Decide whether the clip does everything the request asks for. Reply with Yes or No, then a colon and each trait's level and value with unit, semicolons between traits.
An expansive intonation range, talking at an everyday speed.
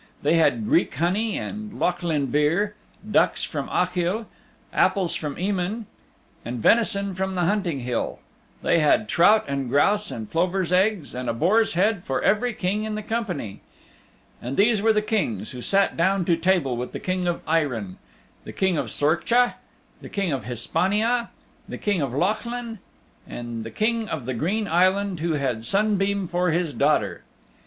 Yes: wide, 6.3 semitones; average, 165 wpm